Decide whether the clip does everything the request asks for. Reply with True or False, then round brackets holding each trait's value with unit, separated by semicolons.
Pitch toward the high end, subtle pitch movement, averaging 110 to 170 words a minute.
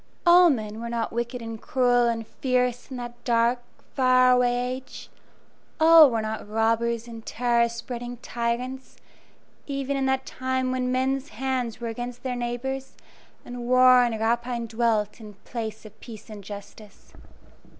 True (240 Hz; 1.9 semitones; 150 wpm)